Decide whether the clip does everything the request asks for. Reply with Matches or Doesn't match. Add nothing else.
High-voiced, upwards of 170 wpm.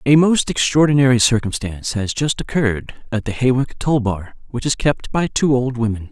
Doesn't match